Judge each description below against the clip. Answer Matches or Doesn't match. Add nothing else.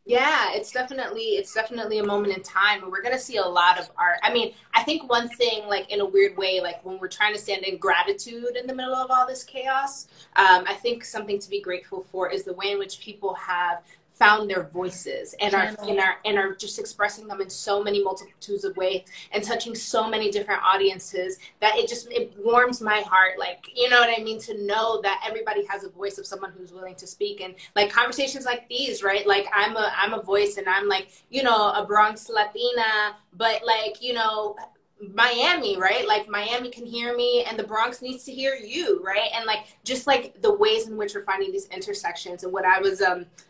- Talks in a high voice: Matches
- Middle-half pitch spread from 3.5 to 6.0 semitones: Matches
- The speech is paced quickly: Matches